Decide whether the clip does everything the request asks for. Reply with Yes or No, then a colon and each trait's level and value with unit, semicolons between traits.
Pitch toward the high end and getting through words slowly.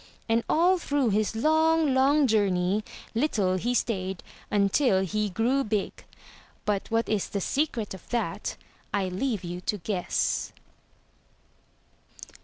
Yes: high, 215 Hz; slow, 125 wpm